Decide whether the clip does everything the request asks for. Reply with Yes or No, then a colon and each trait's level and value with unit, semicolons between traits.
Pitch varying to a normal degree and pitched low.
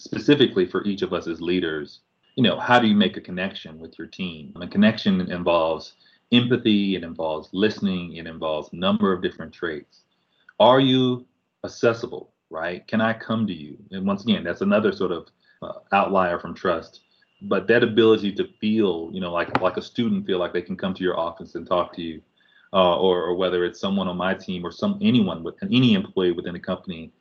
No: wide, 6.4 semitones; low, 105 Hz